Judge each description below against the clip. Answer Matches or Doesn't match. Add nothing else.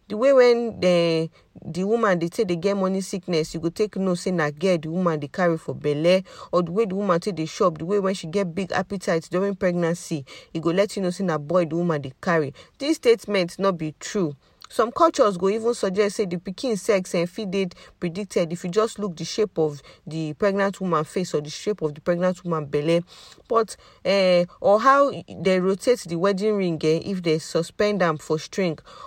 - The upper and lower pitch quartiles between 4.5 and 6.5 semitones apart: Doesn't match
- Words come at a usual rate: Doesn't match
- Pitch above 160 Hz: Matches